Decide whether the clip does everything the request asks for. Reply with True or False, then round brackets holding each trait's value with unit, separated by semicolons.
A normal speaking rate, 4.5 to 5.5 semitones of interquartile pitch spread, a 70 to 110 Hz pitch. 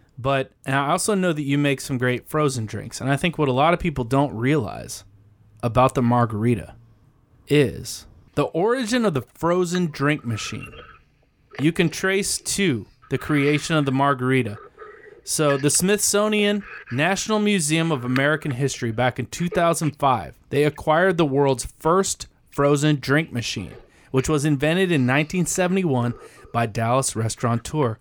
False (150 wpm; 5.1 semitones; 140 Hz)